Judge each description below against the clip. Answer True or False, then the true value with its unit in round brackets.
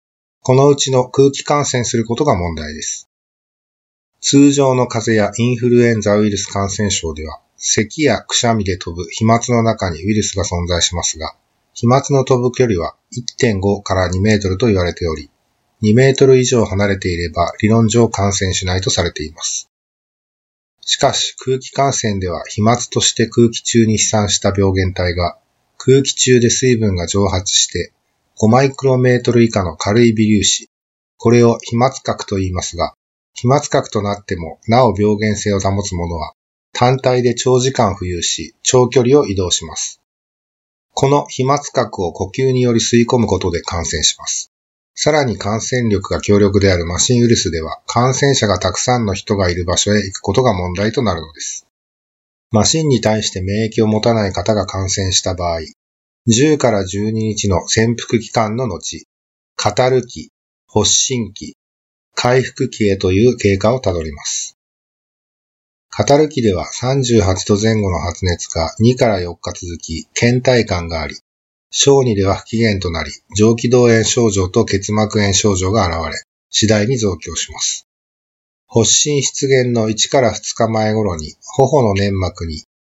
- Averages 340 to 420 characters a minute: False (300 characters per minute)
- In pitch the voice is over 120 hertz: False (105 Hz)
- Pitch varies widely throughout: False (4.7 semitones)